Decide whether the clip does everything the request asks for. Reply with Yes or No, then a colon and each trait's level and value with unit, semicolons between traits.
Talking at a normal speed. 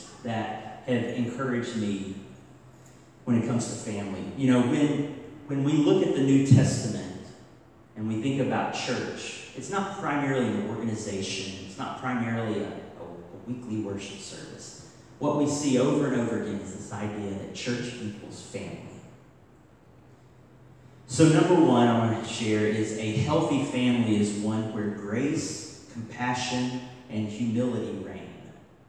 Yes: average, 145 wpm